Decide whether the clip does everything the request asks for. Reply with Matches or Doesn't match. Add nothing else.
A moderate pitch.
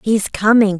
Doesn't match